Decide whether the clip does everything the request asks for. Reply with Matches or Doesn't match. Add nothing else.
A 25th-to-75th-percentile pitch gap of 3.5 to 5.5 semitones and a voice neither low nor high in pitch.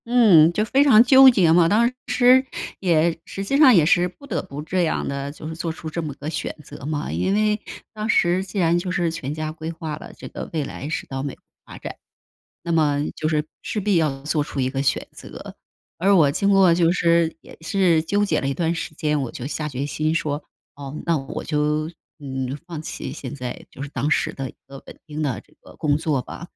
Matches